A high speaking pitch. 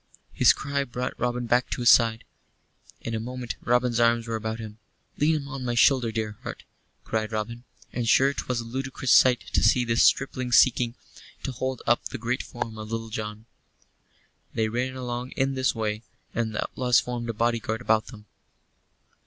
No: low, 120 Hz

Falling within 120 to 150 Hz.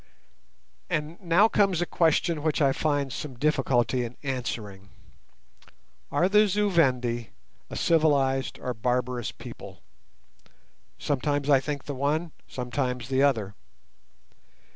Yes: medium, 140 Hz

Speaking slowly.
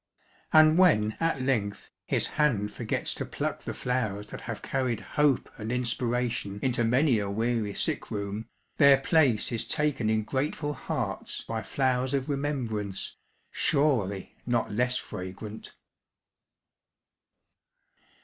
Yes: slow, 125 wpm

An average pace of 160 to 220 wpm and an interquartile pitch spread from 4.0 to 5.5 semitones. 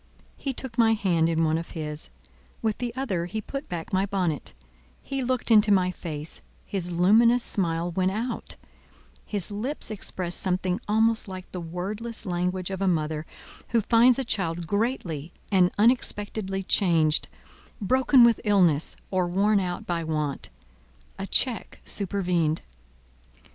No: average, 145 wpm; average, 4.4 semitones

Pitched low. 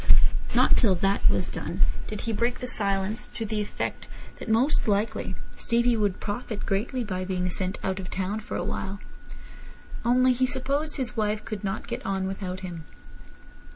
No: high, 210 Hz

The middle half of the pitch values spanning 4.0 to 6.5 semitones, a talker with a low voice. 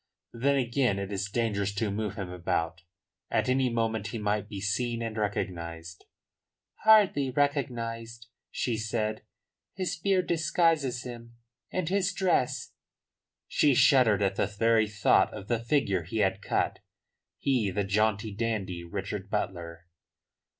Yes: average, 4.3 semitones; low, 110 Hz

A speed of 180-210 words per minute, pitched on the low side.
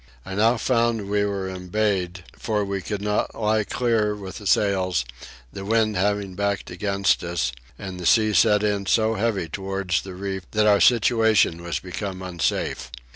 No: average, 170 wpm; low, 100 Hz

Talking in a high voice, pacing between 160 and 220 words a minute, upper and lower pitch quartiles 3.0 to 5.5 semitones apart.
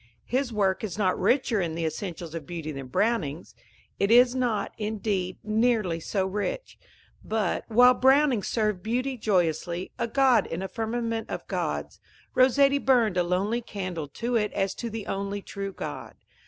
Yes: high, 210 Hz; average, 165 wpm; average, 4.6 semitones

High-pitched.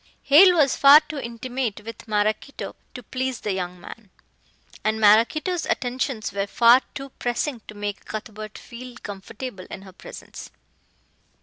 Yes: high, 235 Hz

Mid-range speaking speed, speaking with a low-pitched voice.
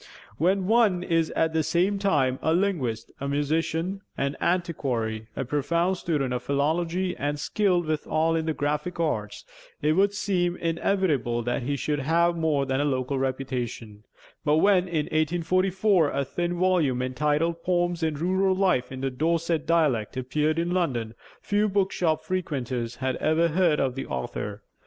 No: average, 160 wpm; medium, 160 Hz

